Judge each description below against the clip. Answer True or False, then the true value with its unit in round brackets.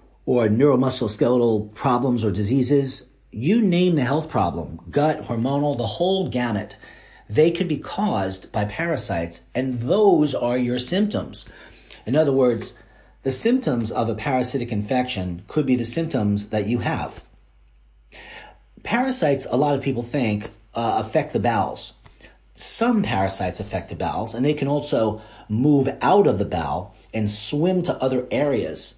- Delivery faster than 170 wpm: False (145 wpm)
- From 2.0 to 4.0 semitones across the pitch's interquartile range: False (5.4 semitones)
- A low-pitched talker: True (120 Hz)